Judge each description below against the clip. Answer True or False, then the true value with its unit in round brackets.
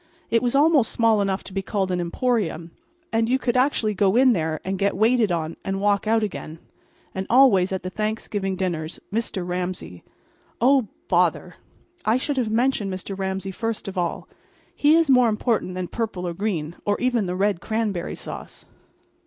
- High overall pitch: True (205 Hz)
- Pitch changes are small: False (4.0 semitones)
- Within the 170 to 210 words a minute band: True (180 wpm)